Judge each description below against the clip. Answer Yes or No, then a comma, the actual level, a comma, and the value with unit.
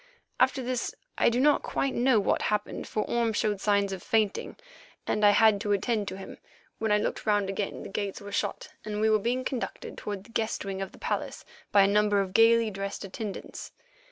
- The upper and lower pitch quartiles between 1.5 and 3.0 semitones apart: Yes, narrow, 2.4 semitones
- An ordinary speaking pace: No, fast, 210 wpm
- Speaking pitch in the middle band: No, high, 210 Hz